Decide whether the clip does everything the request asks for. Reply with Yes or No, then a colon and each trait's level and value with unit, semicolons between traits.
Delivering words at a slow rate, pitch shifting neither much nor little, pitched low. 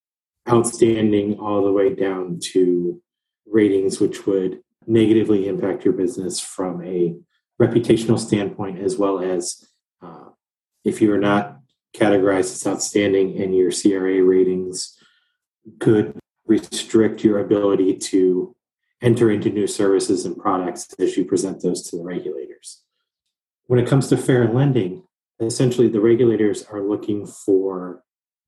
Yes: slow, 130 wpm; average, 3.9 semitones; low, 105 Hz